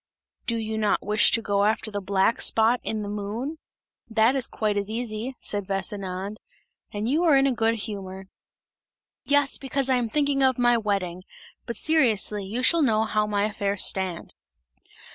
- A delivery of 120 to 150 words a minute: No, average, 170 wpm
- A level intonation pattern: No, average, 3.5 semitones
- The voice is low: No, high, 220 Hz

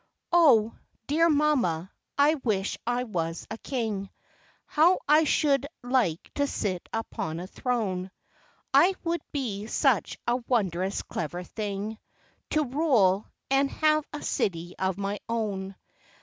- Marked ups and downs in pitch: Yes, wide, 6.9 semitones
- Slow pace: Yes, slow, 130 wpm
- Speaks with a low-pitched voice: No, high, 225 Hz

